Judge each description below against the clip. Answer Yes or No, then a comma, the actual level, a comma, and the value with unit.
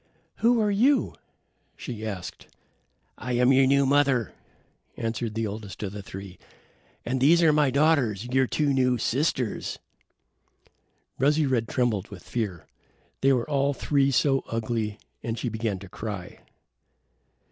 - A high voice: No, low, 125 Hz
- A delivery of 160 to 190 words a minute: No, average, 140 wpm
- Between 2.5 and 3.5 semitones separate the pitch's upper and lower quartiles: No, average, 4.3 semitones